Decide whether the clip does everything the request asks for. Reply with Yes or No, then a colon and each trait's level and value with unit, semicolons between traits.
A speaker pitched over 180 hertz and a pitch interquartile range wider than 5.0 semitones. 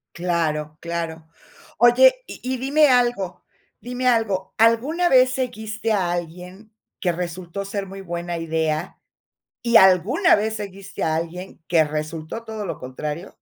Yes: high, 190 Hz; wide, 5.4 semitones